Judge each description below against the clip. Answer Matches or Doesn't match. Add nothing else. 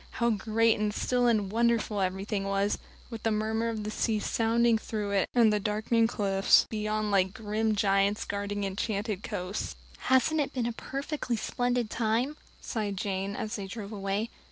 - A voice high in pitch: Matches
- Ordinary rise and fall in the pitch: Doesn't match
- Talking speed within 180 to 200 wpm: Doesn't match